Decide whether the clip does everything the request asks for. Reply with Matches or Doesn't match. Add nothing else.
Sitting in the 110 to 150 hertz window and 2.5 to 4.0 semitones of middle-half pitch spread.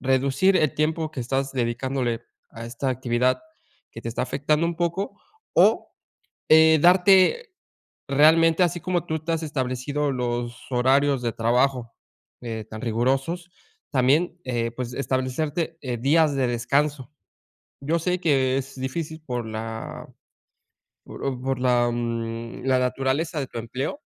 Doesn't match